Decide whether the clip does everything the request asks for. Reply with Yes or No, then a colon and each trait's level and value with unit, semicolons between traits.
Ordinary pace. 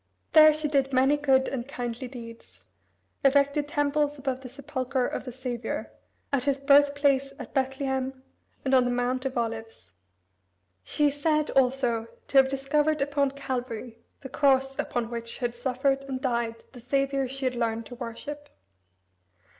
Yes: average, 155 wpm